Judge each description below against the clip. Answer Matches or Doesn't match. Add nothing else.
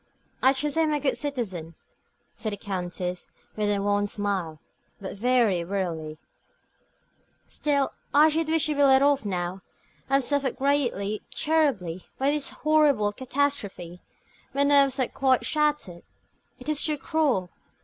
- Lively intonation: Matches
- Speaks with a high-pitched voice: Matches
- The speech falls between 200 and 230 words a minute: Doesn't match